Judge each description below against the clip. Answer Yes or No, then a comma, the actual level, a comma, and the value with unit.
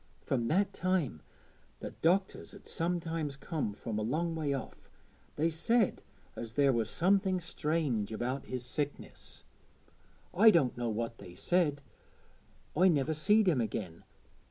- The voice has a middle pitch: Yes, medium, 150 Hz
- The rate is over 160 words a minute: No, average, 140 wpm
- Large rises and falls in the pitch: Yes, wide, 6.4 semitones